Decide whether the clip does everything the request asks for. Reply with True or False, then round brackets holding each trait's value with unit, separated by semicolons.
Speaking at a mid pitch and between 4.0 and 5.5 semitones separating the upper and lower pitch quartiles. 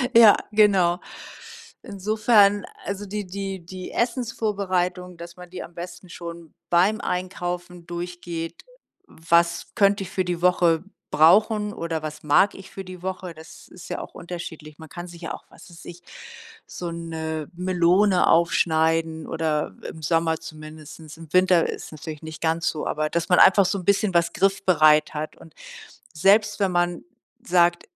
False (175 Hz; 2.6 semitones)